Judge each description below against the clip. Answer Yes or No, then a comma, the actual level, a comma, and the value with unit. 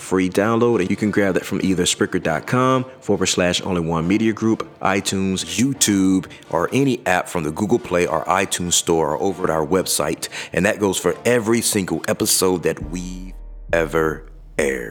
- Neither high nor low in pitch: No, very low, 95 Hz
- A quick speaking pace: No, average, 175 wpm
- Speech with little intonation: No, average, 3.1 semitones